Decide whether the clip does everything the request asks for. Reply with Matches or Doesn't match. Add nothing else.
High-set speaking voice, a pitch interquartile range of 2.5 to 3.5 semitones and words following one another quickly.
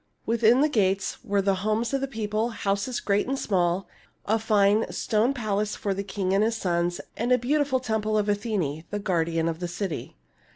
Doesn't match